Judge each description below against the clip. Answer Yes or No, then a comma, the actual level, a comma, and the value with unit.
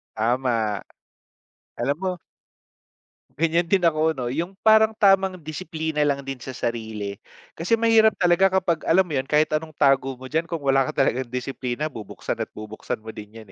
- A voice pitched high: No, medium, 150 Hz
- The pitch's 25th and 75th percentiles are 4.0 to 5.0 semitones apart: No, wide, 5.5 semitones